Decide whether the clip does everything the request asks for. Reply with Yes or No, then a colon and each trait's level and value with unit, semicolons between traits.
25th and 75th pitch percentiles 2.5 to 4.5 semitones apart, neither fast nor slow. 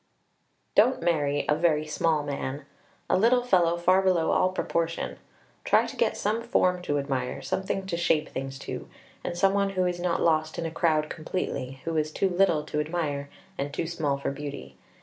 Yes: average, 3.8 semitones; average, 190 wpm